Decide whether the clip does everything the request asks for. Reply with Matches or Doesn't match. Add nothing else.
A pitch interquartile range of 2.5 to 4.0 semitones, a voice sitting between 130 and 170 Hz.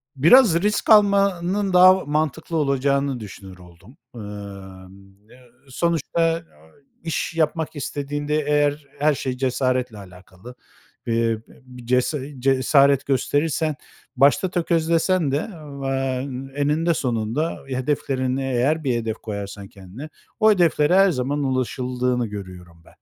Doesn't match